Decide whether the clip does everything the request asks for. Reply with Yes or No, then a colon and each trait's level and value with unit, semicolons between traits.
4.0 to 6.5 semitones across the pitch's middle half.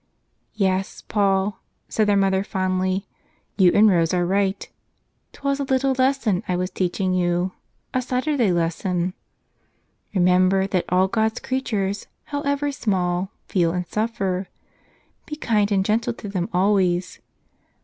No: average, 3.2 semitones